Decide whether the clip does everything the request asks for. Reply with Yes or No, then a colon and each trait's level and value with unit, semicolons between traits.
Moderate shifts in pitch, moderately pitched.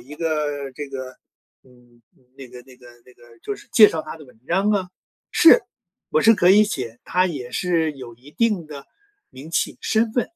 No: wide, 6.3 semitones; medium, 150 Hz